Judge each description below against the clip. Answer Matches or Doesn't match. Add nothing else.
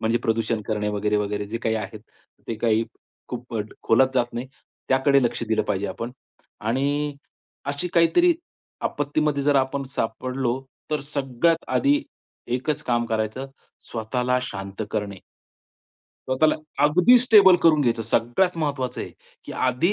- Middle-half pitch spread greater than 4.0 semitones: Matches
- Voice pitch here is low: Matches